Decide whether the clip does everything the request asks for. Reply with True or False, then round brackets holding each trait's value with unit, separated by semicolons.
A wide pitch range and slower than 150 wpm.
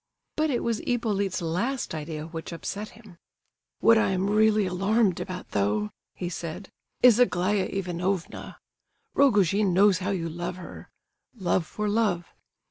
False (3.7 semitones; 140 wpm)